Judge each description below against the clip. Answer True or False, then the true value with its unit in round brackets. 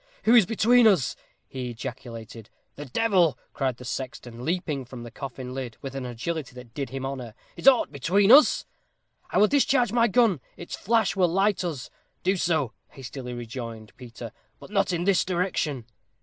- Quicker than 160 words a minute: True (175 wpm)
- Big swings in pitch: True (7.8 semitones)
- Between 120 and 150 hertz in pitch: True (140 Hz)